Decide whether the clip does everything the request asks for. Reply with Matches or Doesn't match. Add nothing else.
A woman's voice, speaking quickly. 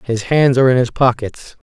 Doesn't match